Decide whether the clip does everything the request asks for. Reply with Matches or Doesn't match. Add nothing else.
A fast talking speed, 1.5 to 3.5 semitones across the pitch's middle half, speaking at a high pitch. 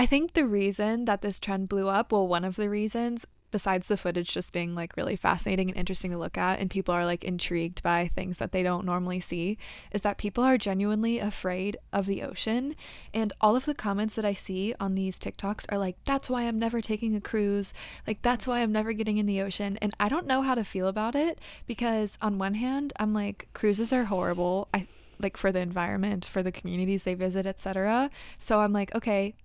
Matches